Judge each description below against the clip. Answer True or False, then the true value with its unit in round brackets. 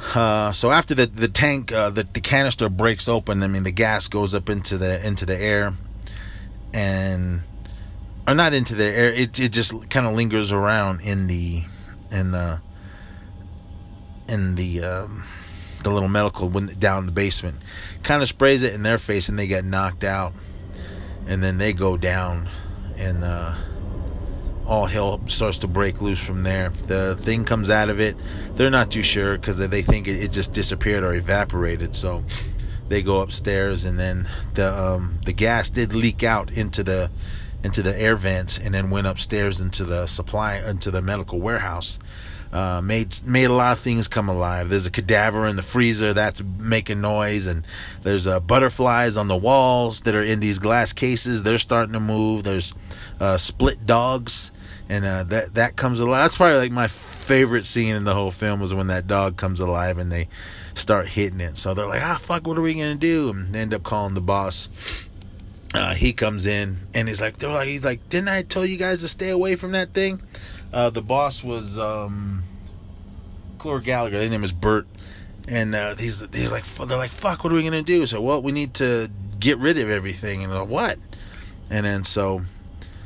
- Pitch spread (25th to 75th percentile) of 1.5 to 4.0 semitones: True (3.4 semitones)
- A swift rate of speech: False (195 wpm)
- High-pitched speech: False (100 Hz)